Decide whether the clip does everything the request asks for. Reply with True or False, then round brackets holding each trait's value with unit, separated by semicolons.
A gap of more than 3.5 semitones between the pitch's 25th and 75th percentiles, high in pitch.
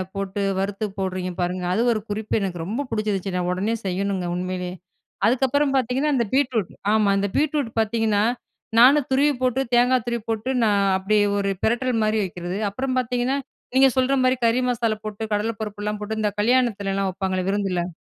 True (4.2 semitones; 215 Hz)